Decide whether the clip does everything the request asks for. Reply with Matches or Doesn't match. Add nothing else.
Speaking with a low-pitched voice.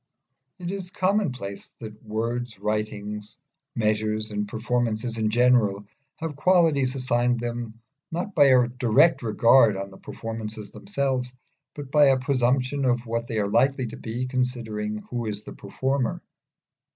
Matches